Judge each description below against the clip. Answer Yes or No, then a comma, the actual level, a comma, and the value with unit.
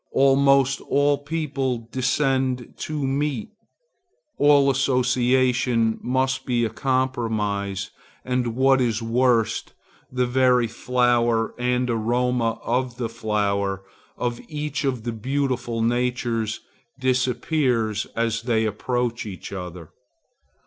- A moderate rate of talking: No, slow, 105 wpm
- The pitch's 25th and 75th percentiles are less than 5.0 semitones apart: Yes, narrow, 2.5 semitones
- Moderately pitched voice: No, low, 125 Hz